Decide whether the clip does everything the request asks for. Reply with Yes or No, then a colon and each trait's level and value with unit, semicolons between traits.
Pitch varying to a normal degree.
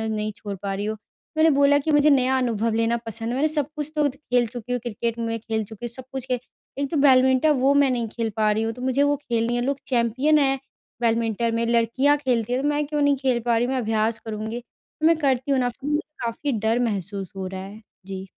Yes: average, 3.7 semitones